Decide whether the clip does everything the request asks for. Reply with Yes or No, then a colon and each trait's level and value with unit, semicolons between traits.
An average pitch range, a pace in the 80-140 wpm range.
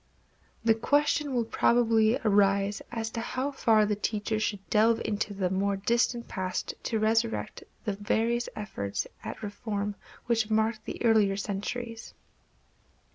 No: narrow, 2.2 semitones; slow, 135 wpm